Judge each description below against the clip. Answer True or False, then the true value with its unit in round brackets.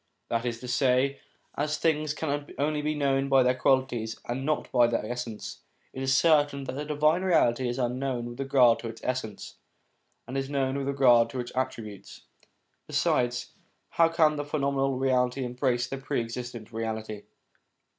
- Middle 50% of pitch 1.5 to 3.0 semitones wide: True (2.7 semitones)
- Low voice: True (130 Hz)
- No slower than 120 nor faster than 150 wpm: False (170 wpm)